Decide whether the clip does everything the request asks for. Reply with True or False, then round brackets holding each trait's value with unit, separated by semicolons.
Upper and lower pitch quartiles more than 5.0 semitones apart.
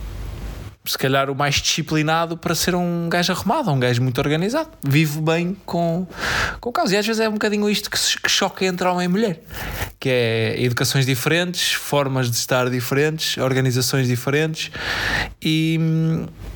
True (5.5 semitones)